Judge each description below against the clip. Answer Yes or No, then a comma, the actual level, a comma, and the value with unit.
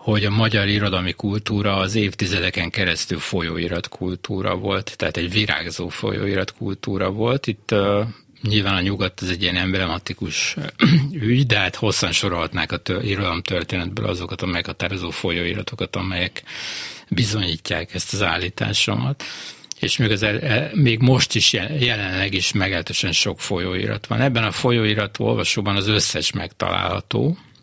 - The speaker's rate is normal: Yes, average, 135 wpm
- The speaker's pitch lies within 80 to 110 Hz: Yes, low, 100 Hz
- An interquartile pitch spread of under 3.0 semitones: No, average, 3.4 semitones